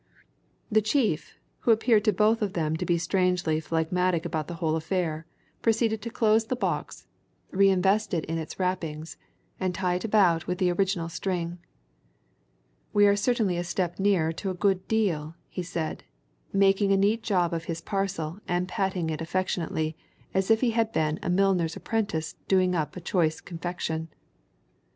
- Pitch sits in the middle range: Yes, medium, 180 Hz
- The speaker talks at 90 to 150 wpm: No, average, 170 wpm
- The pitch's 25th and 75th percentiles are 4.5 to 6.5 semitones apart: No, average, 3.4 semitones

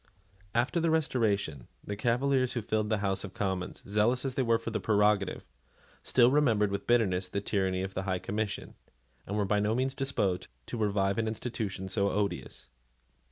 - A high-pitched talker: No, low, 105 Hz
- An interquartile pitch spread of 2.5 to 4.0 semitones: Yes, average, 3.4 semitones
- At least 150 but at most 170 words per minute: No, average, 180 wpm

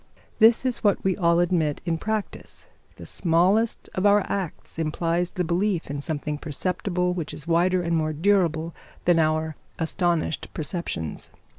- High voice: No, medium, 170 Hz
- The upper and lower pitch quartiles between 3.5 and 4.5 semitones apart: No, average, 2.7 semitones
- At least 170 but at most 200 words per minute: No, average, 150 wpm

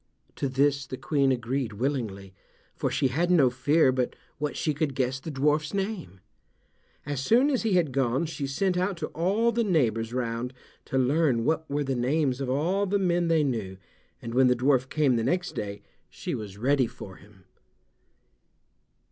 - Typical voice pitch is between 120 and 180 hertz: Yes, low, 135 Hz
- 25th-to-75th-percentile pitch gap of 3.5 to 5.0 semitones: Yes, average, 4.6 semitones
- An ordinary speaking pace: Yes, average, 180 wpm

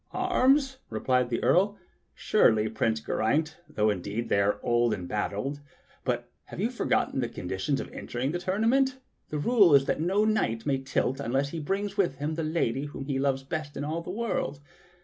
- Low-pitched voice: No, medium, 145 Hz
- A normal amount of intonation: No, wide, 8.2 semitones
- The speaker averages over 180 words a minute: Yes, average, 190 wpm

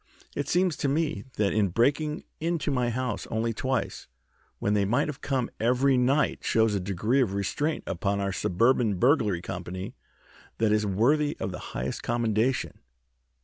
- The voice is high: No, low, 115 Hz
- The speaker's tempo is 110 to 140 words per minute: No, average, 160 wpm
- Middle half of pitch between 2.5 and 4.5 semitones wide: No, wide, 5.4 semitones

